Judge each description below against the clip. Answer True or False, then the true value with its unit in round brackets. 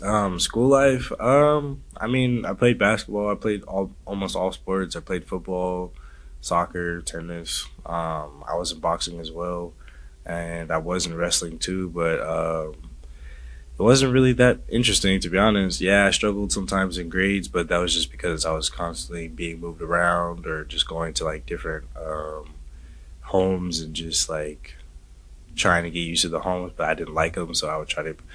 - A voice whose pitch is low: True (85 Hz)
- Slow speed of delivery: False (185 wpm)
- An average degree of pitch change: True (3.1 semitones)